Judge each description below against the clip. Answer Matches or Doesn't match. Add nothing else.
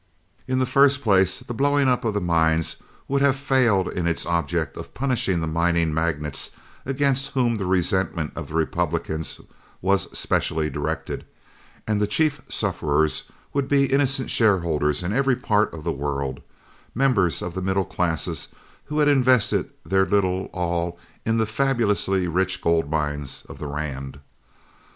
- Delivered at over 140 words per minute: Matches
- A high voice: Doesn't match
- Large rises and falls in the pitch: Matches